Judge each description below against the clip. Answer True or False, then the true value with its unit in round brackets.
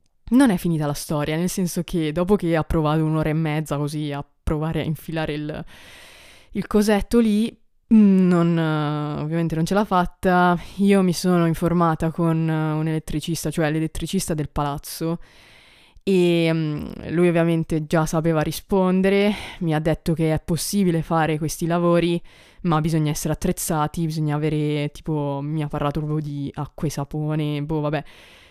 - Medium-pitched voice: True (160 Hz)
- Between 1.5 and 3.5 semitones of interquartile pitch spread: True (2.5 semitones)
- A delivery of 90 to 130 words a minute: False (155 wpm)